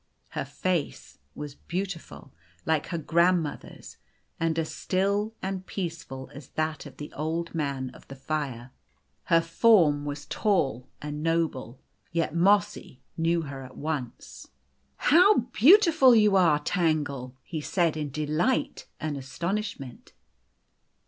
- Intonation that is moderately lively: Yes, average, 4.4 semitones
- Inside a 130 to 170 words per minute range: Yes, slow, 135 wpm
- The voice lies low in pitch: No, medium, 160 Hz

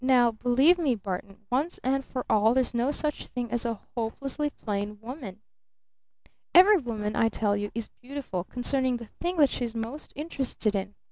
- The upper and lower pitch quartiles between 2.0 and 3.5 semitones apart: No, average, 4.1 semitones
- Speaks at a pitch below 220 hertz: No, high, 245 Hz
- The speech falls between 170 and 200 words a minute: Yes, average, 180 wpm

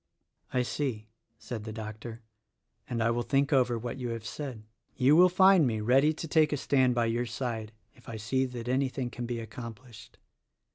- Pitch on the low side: Yes, low, 120 Hz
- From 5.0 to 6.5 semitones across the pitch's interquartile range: No, average, 2.8 semitones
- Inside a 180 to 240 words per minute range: Yes, average, 190 wpm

